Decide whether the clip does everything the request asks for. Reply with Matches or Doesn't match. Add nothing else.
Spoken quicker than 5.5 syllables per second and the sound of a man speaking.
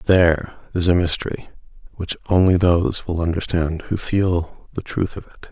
Doesn't match